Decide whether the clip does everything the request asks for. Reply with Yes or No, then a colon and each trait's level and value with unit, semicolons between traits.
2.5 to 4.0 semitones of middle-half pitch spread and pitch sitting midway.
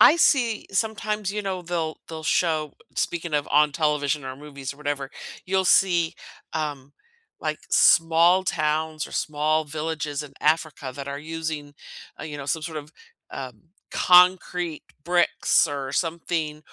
Yes: average, 2.9 semitones; medium, 155 Hz